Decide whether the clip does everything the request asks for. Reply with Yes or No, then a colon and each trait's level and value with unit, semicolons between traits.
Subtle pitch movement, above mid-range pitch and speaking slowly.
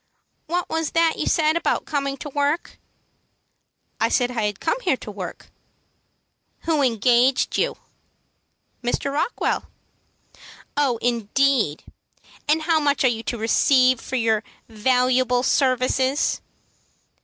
No: average, 3.4 semitones; very high, 260 Hz; slow, 120 wpm